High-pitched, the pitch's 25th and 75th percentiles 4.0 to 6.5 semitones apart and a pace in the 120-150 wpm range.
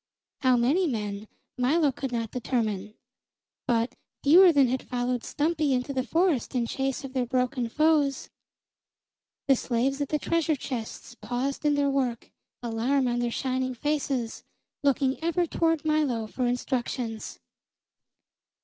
No: very high, 260 Hz; average, 3.2 semitones; average, 140 wpm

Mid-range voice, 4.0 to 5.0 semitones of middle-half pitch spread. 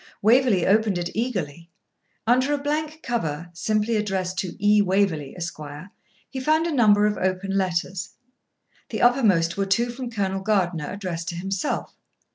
No: high, 195 Hz; average, 4.7 semitones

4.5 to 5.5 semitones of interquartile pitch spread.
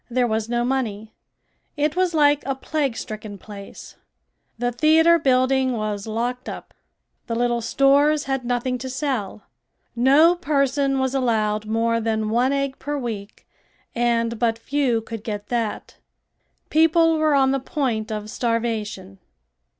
No: average, 3.8 semitones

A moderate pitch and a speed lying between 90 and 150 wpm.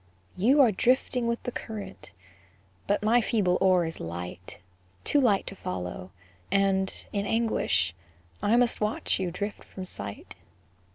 No: high, 200 Hz; average, 140 wpm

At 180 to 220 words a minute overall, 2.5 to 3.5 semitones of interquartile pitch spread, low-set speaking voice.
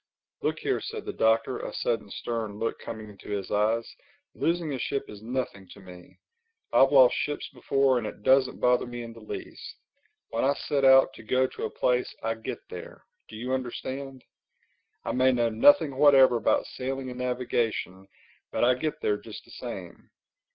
Yes: average, 185 wpm; average, 3.0 semitones; low, 125 Hz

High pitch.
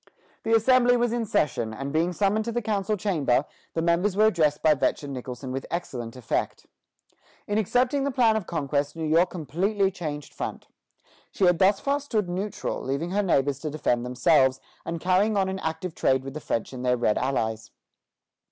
No: medium, 170 Hz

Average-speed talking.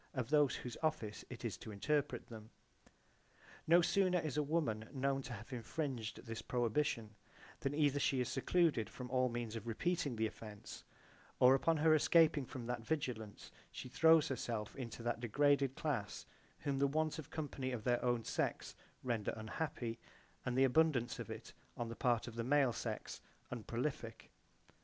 Yes: average, 175 wpm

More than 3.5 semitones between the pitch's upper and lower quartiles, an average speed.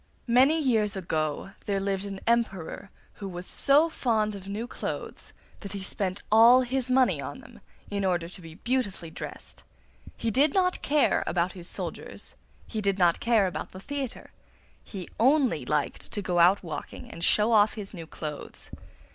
Yes: average, 4.7 semitones; average, 170 wpm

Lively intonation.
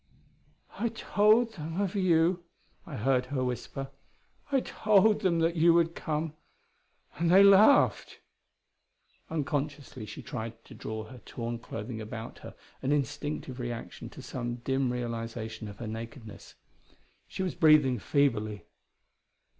Yes: wide, 6.4 semitones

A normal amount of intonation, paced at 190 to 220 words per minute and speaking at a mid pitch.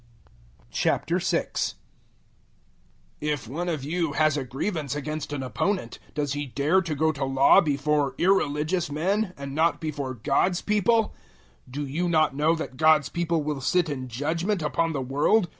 No: average, 3.4 semitones; average, 160 wpm; medium, 150 Hz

